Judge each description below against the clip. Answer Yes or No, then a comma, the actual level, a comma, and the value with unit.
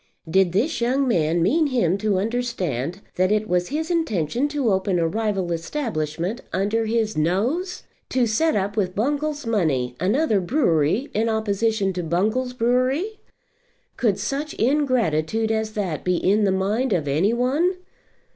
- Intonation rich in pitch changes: Yes, wide, 5.9 semitones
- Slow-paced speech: No, average, 150 wpm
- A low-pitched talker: No, high, 215 Hz